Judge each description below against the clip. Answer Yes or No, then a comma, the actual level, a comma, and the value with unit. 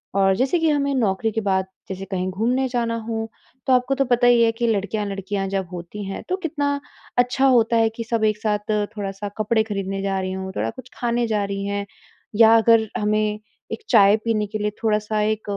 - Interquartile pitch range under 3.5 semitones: Yes, average, 3.1 semitones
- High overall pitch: Yes, high, 215 Hz